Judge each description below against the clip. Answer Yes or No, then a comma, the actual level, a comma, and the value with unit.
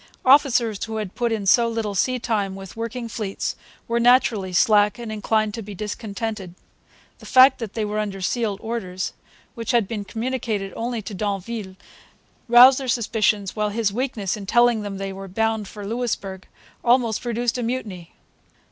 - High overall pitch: Yes, high, 220 Hz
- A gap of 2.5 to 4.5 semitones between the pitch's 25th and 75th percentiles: Yes, average, 3.0 semitones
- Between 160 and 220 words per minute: Yes, average, 170 wpm